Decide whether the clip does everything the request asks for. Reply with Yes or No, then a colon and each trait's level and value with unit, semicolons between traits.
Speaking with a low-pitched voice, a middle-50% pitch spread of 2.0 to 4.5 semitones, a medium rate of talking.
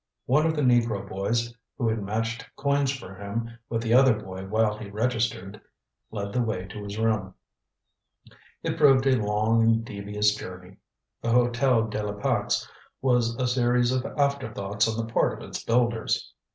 Yes: low, 115 Hz; average, 2.9 semitones; average, 170 wpm